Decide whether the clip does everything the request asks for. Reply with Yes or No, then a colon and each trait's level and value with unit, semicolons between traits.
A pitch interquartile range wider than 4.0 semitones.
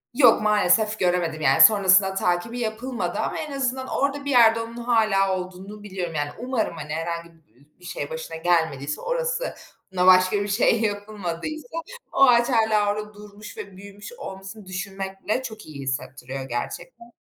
Yes: average, 4.5 semitones